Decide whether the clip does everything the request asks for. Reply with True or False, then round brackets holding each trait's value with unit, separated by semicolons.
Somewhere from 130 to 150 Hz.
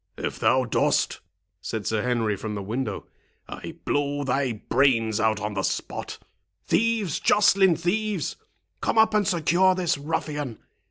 True (140 Hz)